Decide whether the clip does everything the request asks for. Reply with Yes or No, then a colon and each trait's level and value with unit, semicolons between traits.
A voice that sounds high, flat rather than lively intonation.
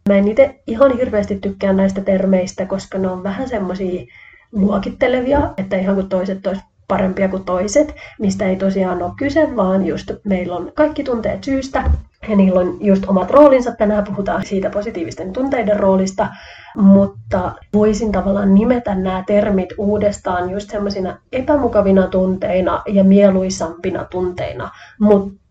Yes: high, 200 Hz; narrow, 2.3 semitones